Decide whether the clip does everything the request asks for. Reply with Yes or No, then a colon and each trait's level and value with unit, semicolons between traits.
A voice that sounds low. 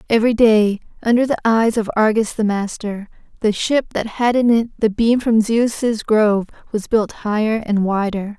No: high, 220 Hz